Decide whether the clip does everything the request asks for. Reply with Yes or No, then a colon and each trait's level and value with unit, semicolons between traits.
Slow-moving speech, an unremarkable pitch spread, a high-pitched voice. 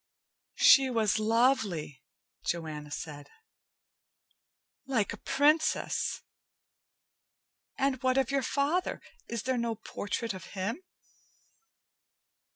No: slow, 90 wpm; wide, 6.0 semitones; high, 230 Hz